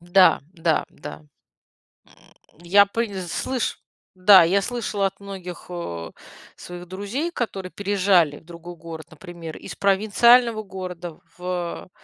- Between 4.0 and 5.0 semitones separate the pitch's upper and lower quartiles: No, average, 2.8 semitones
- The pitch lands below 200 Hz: Yes, medium, 185 Hz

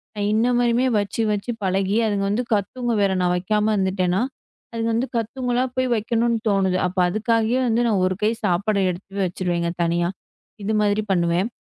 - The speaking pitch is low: No, high, 205 Hz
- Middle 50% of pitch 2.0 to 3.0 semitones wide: No, average, 3.5 semitones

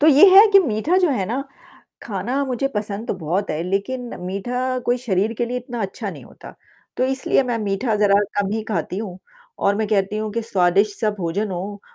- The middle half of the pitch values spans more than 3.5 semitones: Yes, average, 4.1 semitones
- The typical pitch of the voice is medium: No, high, 215 Hz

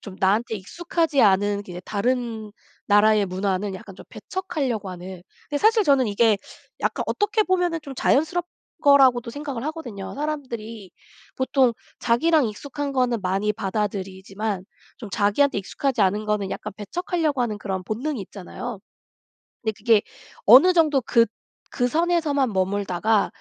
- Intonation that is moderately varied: No, wide, 6.0 semitones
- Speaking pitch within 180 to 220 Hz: No, high, 230 Hz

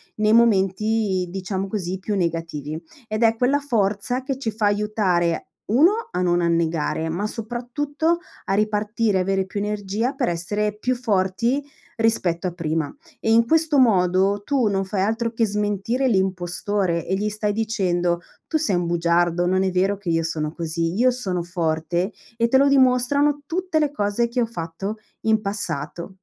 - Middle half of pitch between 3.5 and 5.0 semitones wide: Yes, average, 4.6 semitones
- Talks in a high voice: Yes, high, 205 Hz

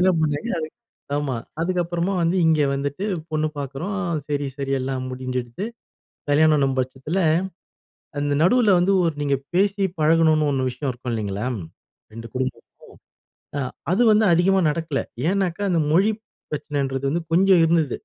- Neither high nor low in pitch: Yes, medium, 155 Hz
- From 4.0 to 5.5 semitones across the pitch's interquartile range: Yes, average, 4.6 semitones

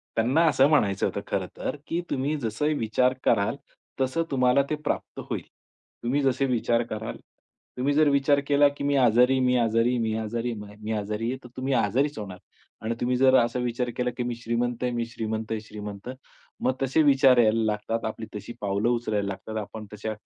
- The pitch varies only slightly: No, average, 3.3 semitones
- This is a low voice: Yes, low, 120 Hz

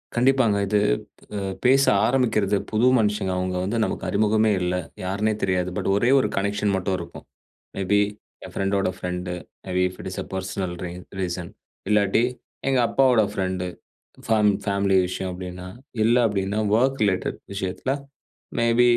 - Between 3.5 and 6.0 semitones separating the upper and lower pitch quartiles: No, average, 3.0 semitones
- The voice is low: Yes, low, 100 Hz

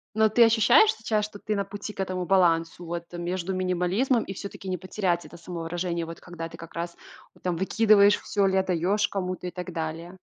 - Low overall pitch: No, medium, 185 Hz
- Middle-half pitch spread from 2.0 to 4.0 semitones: Yes, average, 2.9 semitones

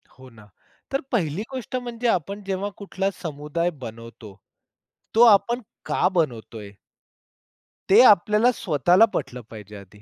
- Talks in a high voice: No, medium, 175 Hz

